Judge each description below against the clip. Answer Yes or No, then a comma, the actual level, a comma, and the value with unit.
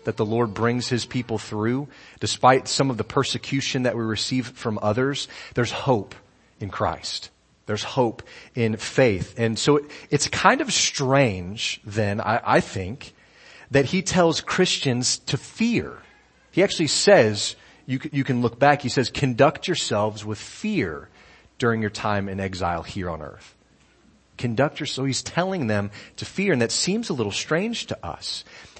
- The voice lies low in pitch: Yes, low, 125 Hz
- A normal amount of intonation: Yes, average, 4.6 semitones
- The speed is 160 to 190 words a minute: Yes, average, 165 wpm